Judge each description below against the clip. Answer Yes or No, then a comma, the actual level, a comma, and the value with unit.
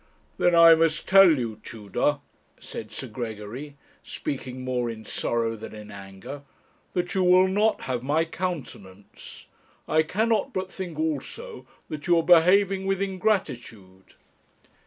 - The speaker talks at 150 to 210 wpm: No, slow, 135 wpm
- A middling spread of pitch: No, wide, 8.2 semitones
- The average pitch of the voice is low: No, medium, 150 Hz